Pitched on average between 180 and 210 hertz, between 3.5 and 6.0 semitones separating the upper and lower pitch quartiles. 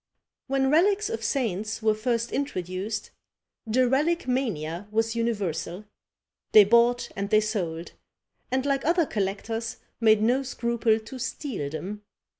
No: high, 225 Hz; average, 3.9 semitones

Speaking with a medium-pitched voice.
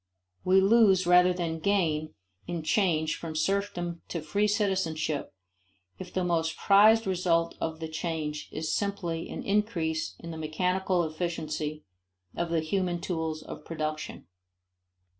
Yes: medium, 170 Hz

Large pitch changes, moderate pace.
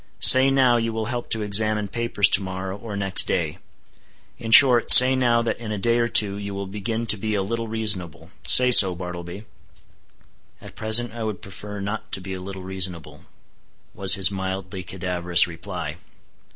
No: average, 3.3 semitones; average, 180 wpm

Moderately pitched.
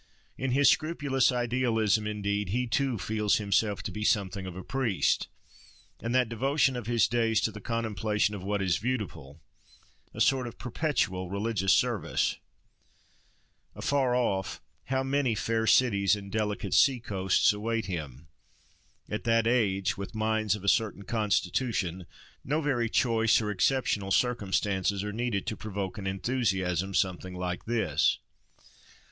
No: low, 110 Hz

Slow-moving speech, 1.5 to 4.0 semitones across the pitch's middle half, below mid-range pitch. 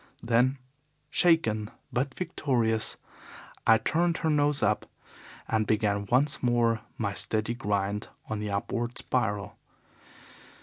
Yes: slow, 115 wpm; average, 3.7 semitones; low, 115 Hz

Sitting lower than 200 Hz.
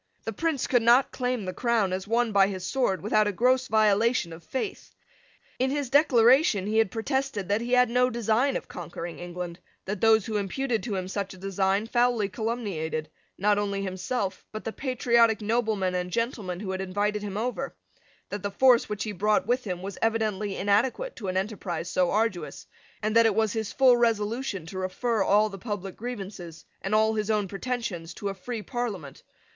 No: high, 215 Hz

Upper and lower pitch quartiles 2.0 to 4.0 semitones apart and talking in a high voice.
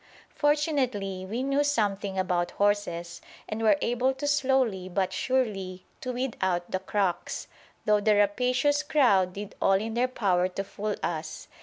No: average, 5.3 semitones; high, 205 Hz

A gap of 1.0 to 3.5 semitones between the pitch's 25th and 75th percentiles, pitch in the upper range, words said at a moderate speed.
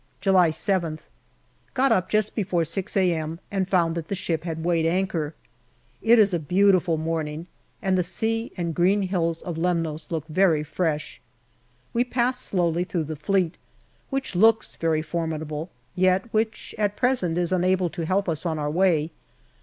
No: average, 3.1 semitones; medium, 175 Hz; average, 165 wpm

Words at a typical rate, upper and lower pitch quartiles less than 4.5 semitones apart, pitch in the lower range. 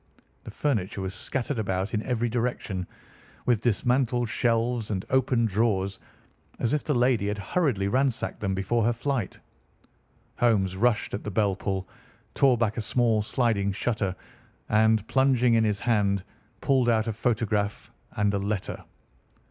Yes: average, 150 wpm; average, 3.3 semitones; low, 110 Hz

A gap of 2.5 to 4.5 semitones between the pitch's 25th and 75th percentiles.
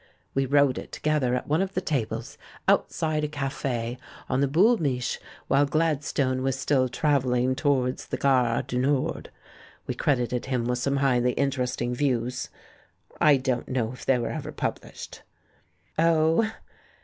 Yes: average, 2.8 semitones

